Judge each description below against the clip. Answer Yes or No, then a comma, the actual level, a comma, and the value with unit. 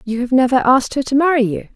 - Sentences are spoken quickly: Yes, fast, 275 wpm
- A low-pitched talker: No, very high, 255 Hz